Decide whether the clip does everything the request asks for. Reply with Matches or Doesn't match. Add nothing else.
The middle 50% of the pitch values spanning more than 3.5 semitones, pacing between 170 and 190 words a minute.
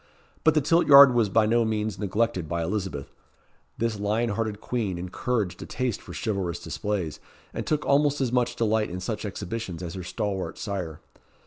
Matches